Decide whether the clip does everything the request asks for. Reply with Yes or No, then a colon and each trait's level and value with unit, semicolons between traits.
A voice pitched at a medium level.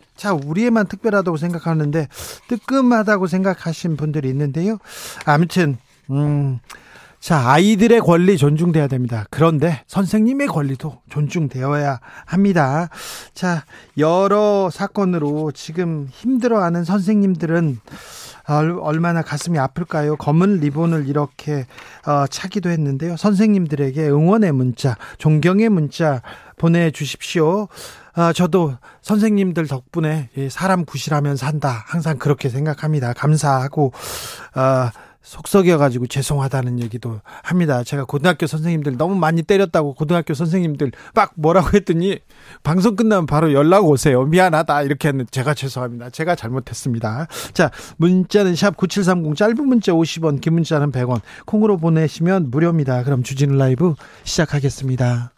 Yes: medium, 155 Hz